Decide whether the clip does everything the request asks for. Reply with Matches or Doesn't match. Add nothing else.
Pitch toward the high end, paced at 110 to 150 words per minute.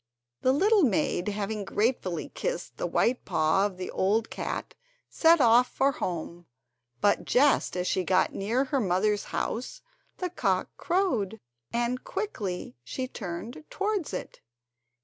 Matches